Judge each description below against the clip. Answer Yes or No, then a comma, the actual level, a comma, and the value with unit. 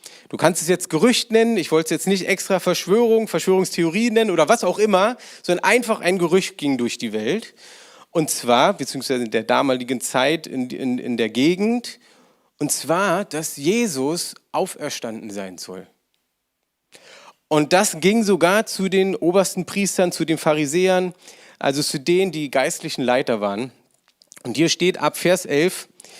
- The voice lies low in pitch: No, medium, 170 Hz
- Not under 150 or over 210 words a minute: Yes, average, 160 wpm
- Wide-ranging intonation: Yes, wide, 5.8 semitones